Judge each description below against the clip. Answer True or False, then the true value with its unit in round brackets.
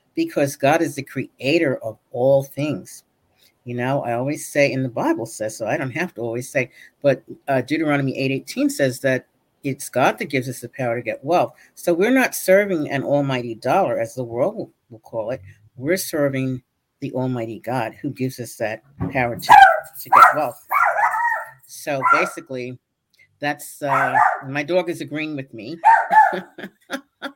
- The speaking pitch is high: False (140 Hz)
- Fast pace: False (170 wpm)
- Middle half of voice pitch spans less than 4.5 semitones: False (4.8 semitones)